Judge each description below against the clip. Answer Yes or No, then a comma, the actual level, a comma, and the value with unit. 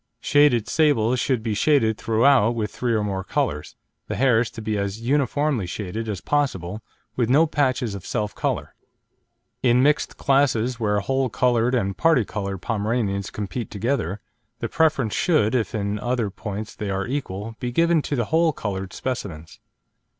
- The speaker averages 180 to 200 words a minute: No, average, 165 wpm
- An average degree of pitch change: Yes, average, 4.5 semitones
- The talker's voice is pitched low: Yes, low, 115 Hz